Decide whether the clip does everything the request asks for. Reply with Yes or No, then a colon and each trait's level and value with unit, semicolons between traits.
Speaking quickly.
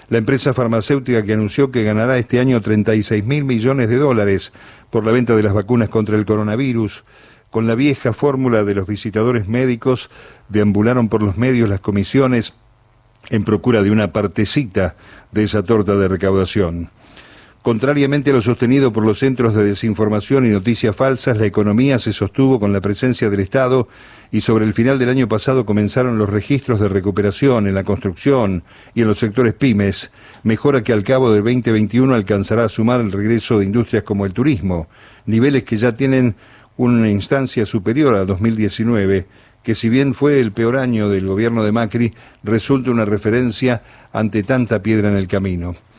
No: average, 175 wpm